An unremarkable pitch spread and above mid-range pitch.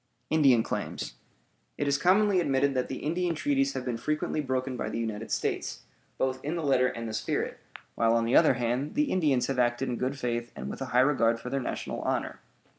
No: average, 3.9 semitones; low, 130 Hz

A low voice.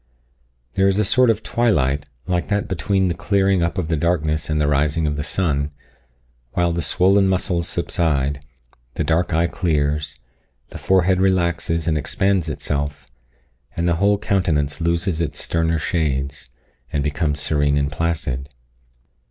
Yes: very low, 85 Hz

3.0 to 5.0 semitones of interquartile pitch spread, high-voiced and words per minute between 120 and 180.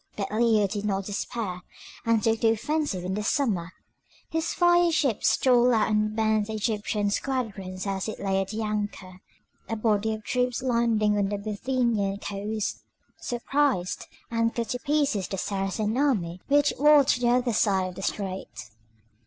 Yes: average, 3.6 semitones; high, 215 Hz; average, 160 wpm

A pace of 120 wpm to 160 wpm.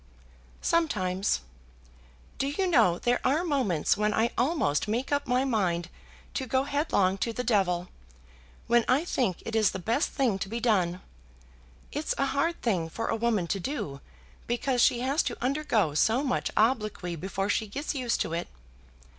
No: average, 170 wpm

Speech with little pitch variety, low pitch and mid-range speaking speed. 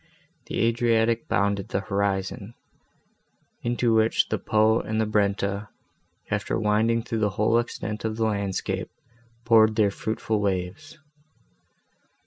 No: narrow, 2.0 semitones; low, 110 Hz; slow, 120 wpm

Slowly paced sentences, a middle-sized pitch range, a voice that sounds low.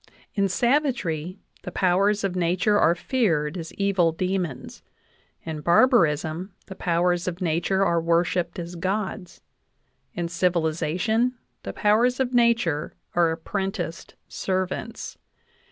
No: slow, 115 wpm; average, 3.3 semitones; medium, 180 Hz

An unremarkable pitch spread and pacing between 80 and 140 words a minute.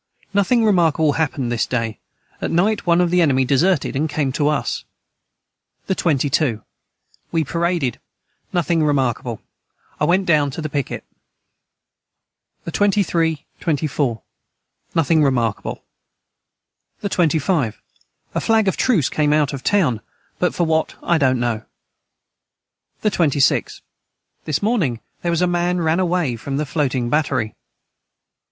Yes: average, 4.6 semitones; slow, 135 wpm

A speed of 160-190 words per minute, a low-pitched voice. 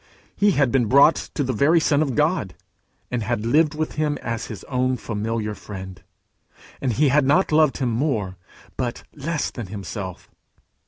Yes: average, 170 wpm; low, 130 Hz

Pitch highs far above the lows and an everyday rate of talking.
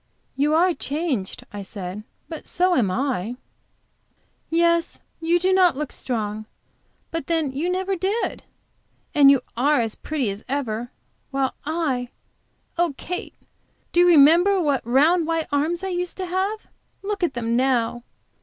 Yes: wide, 6.0 semitones; average, 150 wpm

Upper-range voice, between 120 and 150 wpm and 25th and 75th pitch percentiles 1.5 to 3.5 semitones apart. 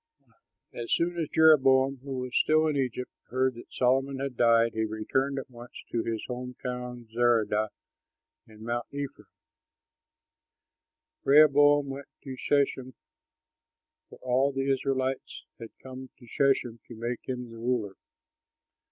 No: low, 130 Hz; slow, 135 wpm; narrow, 2.5 semitones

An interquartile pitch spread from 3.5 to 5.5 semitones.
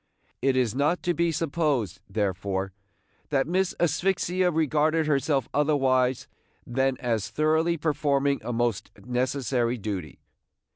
Yes: average, 4.5 semitones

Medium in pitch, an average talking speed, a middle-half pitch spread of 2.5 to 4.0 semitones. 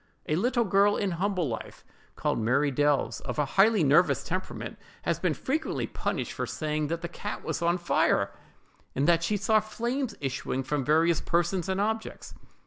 No: medium, 175 Hz; average, 175 wpm; wide, 5.5 semitones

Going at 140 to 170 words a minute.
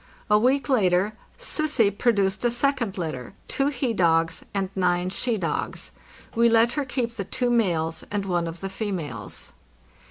Yes: average, 165 wpm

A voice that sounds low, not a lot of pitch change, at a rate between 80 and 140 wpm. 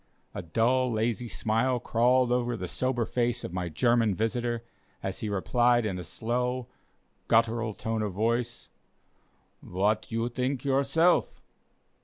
Yes: low, 120 Hz; narrow, 2.3 semitones; slow, 135 wpm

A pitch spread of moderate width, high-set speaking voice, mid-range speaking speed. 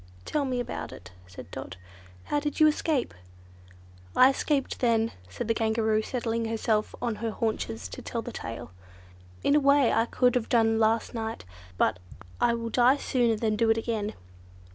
No: narrow, 2.2 semitones; high, 230 Hz; average, 180 wpm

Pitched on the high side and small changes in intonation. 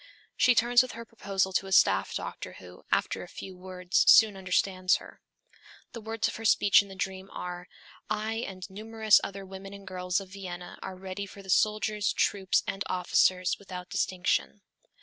Yes: high, 195 Hz; narrow, 2.2 semitones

